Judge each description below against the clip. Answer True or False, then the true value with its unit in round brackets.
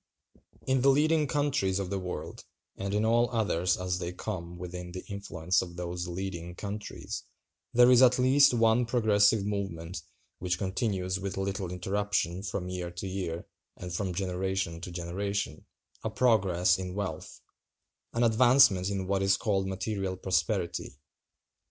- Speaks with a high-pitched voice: False (95 Hz)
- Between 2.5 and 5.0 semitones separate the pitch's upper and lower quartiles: True (3.2 semitones)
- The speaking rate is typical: True (145 wpm)